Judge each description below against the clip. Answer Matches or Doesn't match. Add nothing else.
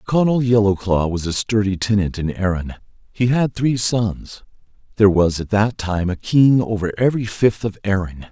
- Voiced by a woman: Doesn't match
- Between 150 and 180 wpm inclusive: Matches